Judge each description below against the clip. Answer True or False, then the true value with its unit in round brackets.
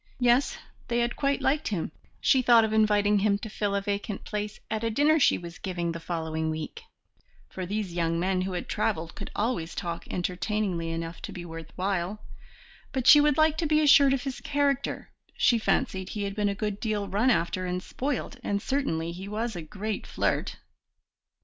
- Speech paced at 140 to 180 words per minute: False (195 wpm)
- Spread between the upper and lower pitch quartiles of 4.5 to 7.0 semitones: True (5.2 semitones)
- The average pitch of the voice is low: False (205 Hz)